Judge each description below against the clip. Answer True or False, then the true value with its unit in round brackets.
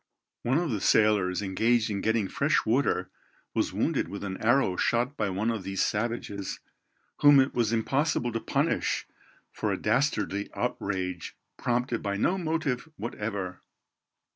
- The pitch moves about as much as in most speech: True (4.1 semitones)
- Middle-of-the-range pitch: False (110 Hz)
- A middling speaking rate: True (145 wpm)